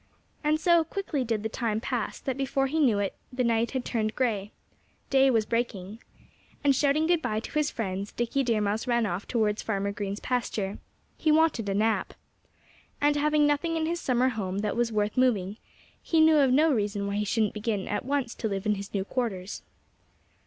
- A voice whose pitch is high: Yes, high, 235 Hz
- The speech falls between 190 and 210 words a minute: Yes, average, 200 wpm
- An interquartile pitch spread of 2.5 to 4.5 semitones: No, average, 5.0 semitones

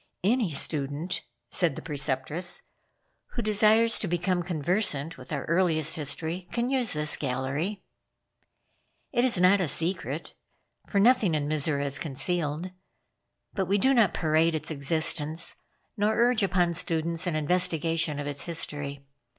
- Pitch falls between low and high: Yes, medium, 165 Hz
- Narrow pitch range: No, average, 4.4 semitones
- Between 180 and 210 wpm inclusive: No, average, 140 wpm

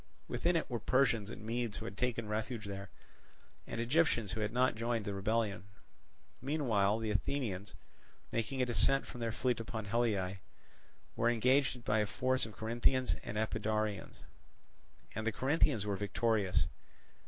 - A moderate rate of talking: Yes, average, 155 wpm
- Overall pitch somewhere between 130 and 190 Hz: No, low, 115 Hz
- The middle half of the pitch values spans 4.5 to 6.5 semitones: No, average, 3.0 semitones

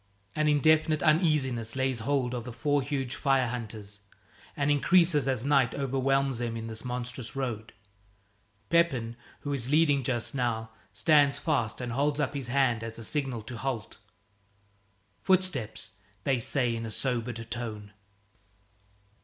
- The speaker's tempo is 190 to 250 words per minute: No, average, 145 wpm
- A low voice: Yes, low, 130 Hz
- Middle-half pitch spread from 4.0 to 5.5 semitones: No, average, 3.6 semitones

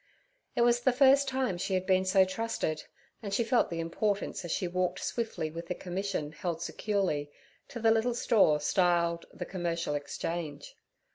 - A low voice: No, medium, 185 Hz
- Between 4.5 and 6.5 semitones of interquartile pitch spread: Yes, average, 5.1 semitones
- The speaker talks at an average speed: Yes, average, 170 wpm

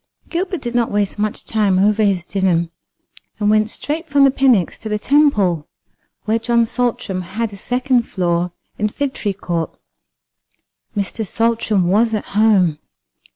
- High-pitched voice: Yes, high, 215 Hz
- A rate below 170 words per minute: Yes, average, 150 wpm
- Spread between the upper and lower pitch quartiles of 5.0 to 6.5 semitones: No, average, 3.9 semitones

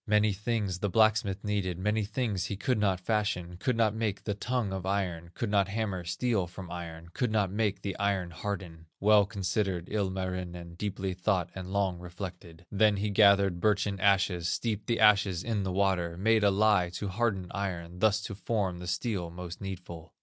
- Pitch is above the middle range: No, low, 100 Hz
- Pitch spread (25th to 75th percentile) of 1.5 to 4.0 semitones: Yes, average, 2.8 semitones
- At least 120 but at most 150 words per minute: No, average, 185 wpm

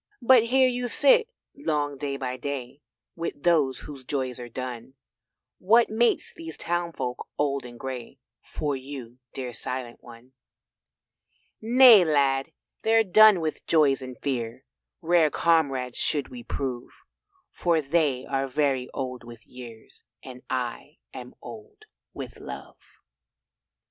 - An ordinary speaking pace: No, slow, 130 wpm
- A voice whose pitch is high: No, medium, 140 Hz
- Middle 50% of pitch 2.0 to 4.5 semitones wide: No, average, 4.9 semitones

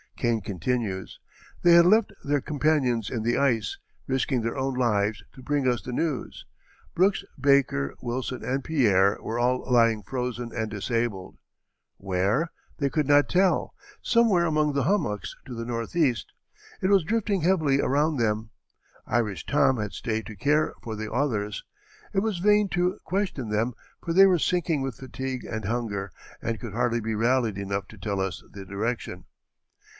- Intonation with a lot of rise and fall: Yes, wide, 5.7 semitones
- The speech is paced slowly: No, average, 165 wpm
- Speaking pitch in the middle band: No, low, 125 Hz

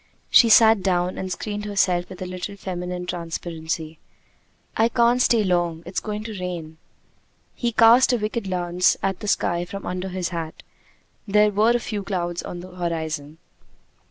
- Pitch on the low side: No, medium, 185 Hz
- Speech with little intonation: No, average, 3.3 semitones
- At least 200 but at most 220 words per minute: No, average, 165 wpm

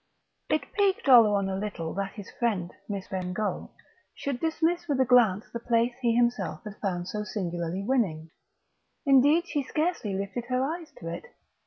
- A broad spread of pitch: Yes, wide, 5.8 semitones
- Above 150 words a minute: Yes, average, 170 wpm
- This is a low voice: No, high, 230 Hz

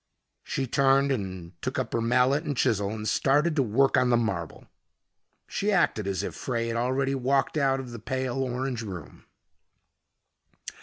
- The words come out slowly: No, average, 160 wpm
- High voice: No, low, 125 Hz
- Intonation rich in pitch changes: No, average, 3.3 semitones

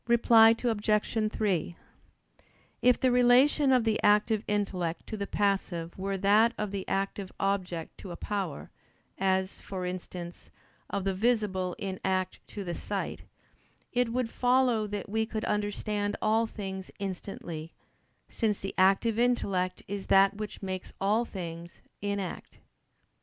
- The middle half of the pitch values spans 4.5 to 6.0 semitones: No, average, 2.8 semitones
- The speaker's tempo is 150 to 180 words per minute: No, average, 140 wpm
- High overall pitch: Yes, high, 200 Hz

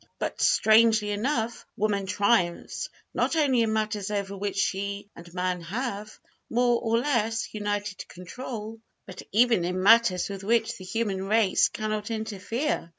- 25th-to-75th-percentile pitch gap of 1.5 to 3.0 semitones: Yes, narrow, 2.6 semitones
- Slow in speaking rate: No, average, 145 wpm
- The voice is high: Yes, high, 210 Hz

